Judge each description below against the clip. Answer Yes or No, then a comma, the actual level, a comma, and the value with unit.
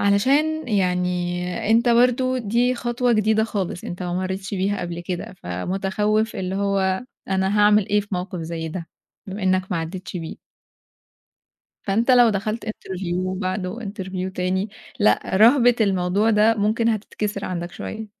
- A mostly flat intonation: No, average, 3.1 semitones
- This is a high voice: Yes, high, 195 Hz